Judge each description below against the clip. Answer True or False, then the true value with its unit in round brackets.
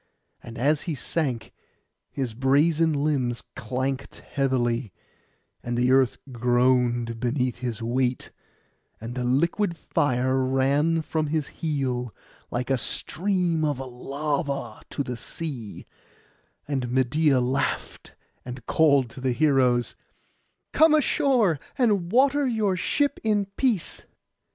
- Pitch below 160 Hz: True (135 Hz)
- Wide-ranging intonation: False (4.4 semitones)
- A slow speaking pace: True (115 wpm)